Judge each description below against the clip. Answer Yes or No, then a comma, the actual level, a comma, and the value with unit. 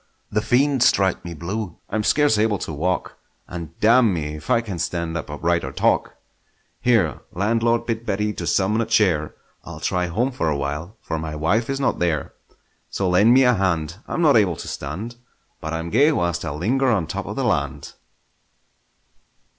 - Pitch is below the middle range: Yes, very low, 95 Hz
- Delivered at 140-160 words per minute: No, average, 185 wpm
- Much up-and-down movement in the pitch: Yes, wide, 5.8 semitones